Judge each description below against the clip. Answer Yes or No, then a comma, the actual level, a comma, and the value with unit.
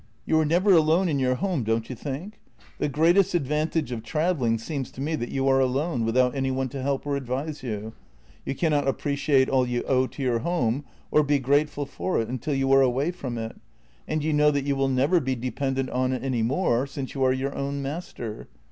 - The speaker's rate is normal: No, fast, 225 wpm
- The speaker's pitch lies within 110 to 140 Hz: Yes, low, 135 Hz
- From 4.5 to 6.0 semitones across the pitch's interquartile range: No, average, 2.9 semitones